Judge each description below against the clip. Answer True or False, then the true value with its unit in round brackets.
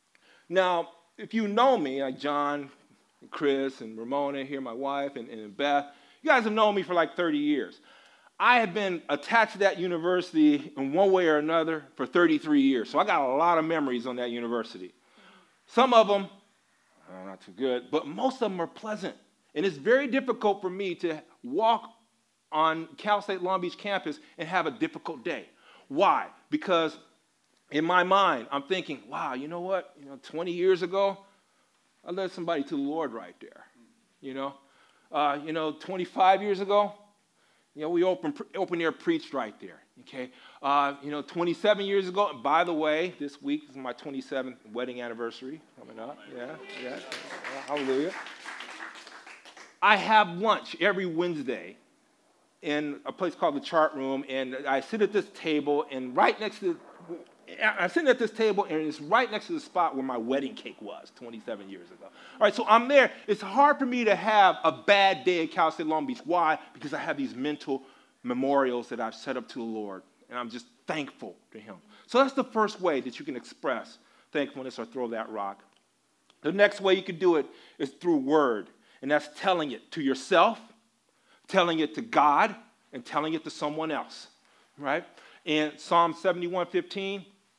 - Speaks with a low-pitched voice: False (175 Hz)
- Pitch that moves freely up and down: True (6.5 semitones)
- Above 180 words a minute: True (190 wpm)